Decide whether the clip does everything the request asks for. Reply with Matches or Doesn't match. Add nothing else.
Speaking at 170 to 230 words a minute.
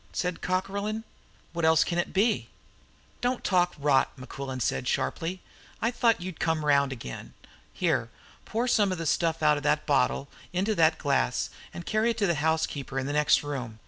Matches